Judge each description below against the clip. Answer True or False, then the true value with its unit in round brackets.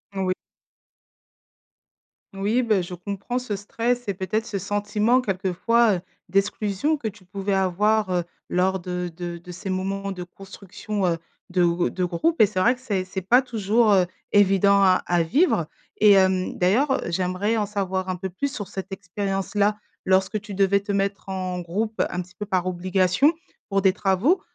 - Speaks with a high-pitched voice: True (195 Hz)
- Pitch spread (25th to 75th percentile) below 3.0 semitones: True (2.4 semitones)